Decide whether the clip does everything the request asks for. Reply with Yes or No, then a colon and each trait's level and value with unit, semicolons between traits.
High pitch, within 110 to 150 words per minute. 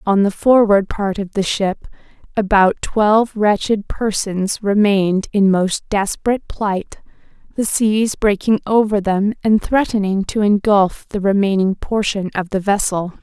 Yes: high, 205 Hz; average, 140 wpm